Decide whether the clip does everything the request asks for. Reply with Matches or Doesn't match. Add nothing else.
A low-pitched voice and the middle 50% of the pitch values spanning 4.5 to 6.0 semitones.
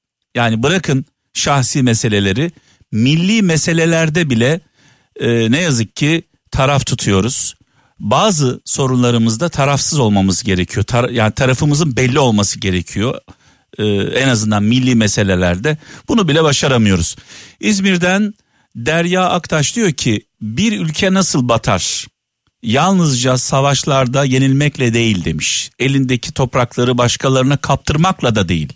Matches